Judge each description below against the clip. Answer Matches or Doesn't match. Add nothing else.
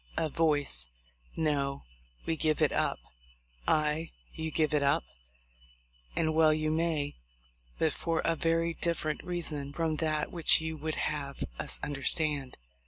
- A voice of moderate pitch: Matches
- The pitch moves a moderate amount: Doesn't match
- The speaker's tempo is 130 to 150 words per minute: Matches